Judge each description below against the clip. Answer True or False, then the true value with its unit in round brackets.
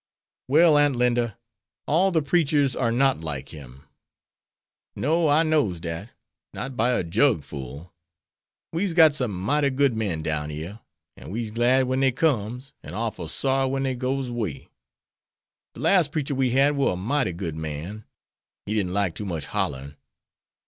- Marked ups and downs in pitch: True (7.7 semitones)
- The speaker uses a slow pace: False (165 wpm)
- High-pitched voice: False (120 Hz)